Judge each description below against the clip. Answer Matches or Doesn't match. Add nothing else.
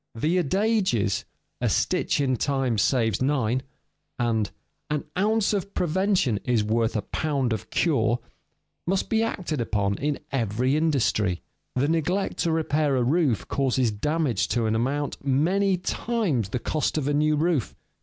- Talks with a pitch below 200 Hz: Matches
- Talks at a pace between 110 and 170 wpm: Matches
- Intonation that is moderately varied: Doesn't match